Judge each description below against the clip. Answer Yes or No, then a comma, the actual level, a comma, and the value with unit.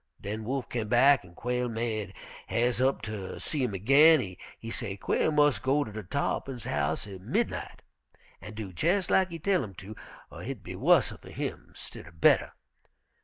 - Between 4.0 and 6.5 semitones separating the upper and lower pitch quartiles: Yes, wide, 5.4 semitones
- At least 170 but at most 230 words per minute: Yes, average, 175 wpm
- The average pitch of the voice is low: Yes, low, 115 Hz